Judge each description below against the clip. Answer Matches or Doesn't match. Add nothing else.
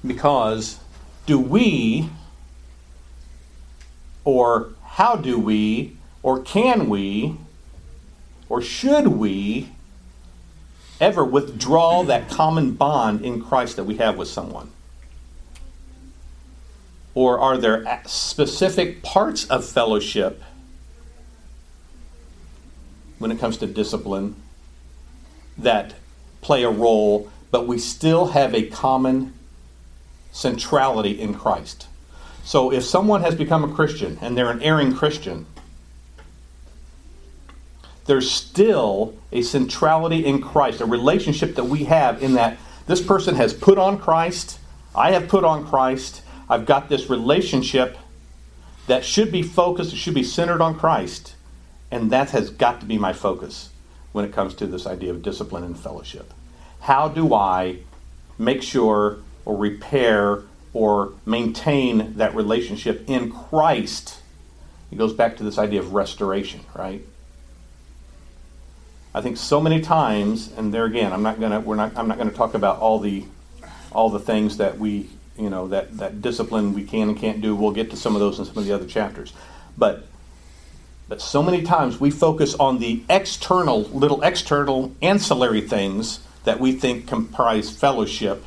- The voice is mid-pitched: Doesn't match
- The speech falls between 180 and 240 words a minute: Doesn't match